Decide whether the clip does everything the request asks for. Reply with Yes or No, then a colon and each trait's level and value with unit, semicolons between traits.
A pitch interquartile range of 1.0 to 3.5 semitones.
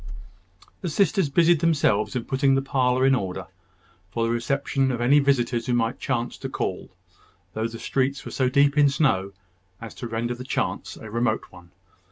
Yes: average, 3.2 semitones